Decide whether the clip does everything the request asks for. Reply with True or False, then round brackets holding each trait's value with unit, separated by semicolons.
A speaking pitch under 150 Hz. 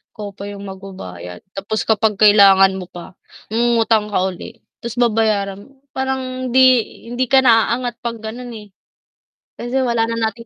False (220 Hz)